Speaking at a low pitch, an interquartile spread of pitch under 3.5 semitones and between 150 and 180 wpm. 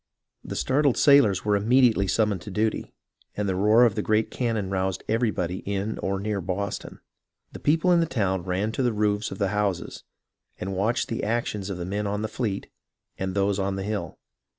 No: low, 105 Hz; narrow, 2.5 semitones; average, 195 wpm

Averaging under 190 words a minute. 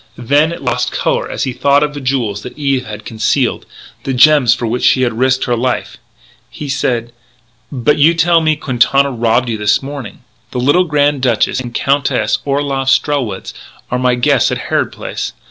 No: average, 195 wpm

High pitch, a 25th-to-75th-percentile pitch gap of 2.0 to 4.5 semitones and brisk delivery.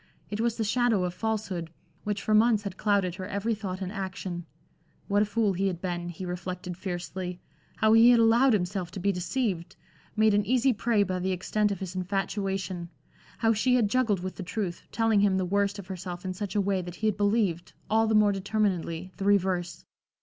Yes: high, 195 Hz; average, 2.9 semitones; fast, 210 wpm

